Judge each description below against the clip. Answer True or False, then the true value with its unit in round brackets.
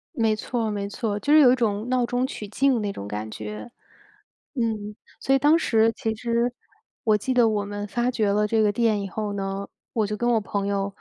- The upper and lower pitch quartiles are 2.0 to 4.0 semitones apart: True (2.9 semitones)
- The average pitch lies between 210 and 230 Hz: True (215 Hz)